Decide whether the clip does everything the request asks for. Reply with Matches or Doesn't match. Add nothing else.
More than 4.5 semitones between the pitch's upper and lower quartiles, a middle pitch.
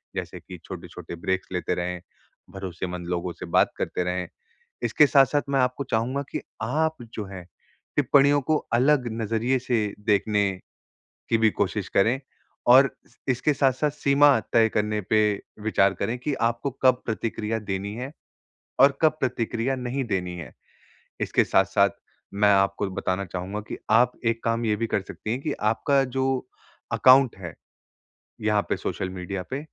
Doesn't match